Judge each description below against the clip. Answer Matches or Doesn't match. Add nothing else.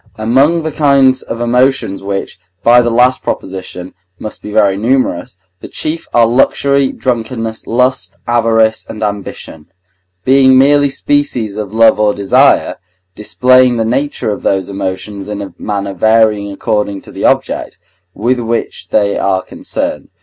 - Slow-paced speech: Doesn't match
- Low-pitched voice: Matches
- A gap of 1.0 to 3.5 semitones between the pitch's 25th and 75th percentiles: Doesn't match